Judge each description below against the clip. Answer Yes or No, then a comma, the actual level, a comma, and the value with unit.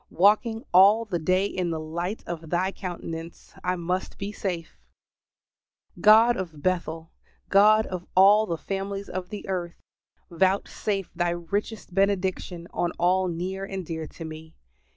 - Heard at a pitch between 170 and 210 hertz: Yes, medium, 185 Hz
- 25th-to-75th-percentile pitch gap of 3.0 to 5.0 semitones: No, narrow, 2.6 semitones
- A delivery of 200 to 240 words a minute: No, average, 145 wpm